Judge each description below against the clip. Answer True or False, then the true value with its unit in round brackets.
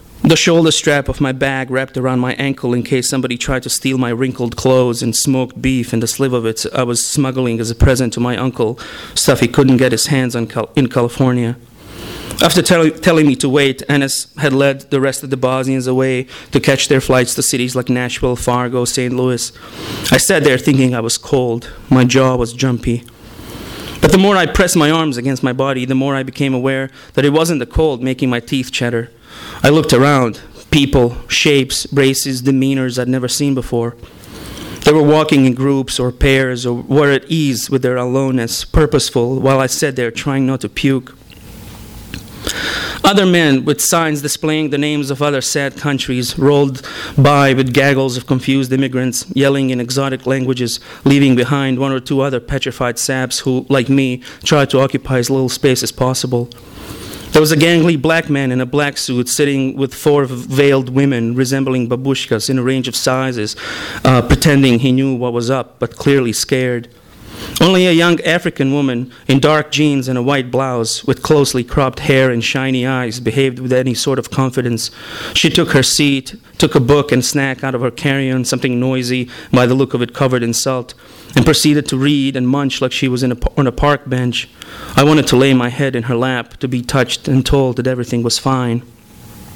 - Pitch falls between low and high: False (130 Hz)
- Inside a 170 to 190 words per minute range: False (200 wpm)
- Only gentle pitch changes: True (2.1 semitones)